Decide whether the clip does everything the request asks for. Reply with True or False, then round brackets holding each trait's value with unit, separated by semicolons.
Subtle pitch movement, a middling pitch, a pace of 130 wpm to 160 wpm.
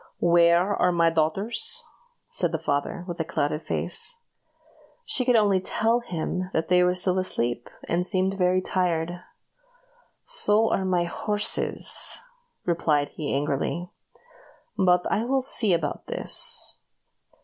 False (3.6 semitones; 180 Hz; 135 wpm)